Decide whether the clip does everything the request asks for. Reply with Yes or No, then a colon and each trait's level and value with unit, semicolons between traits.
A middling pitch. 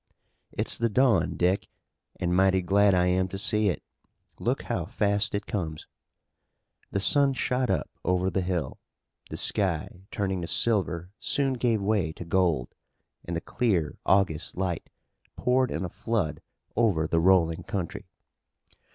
No: very low, 95 Hz